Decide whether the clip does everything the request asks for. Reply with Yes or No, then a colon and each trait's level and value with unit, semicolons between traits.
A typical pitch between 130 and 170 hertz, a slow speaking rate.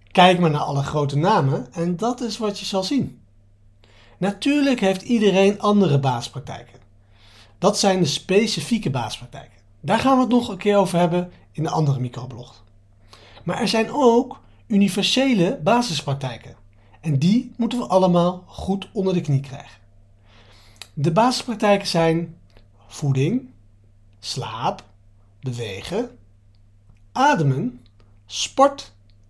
Yes: medium, 140 Hz; slow, 125 wpm